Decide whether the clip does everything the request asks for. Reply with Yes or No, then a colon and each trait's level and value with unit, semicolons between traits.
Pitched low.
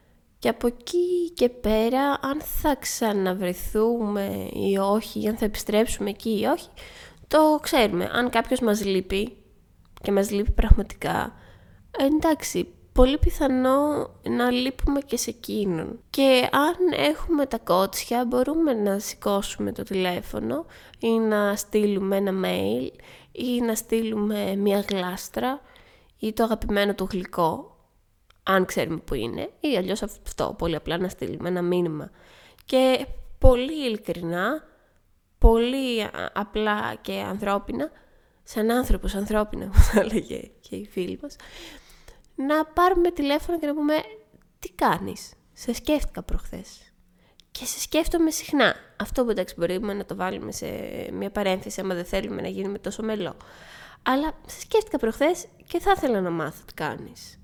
No: high, 225 Hz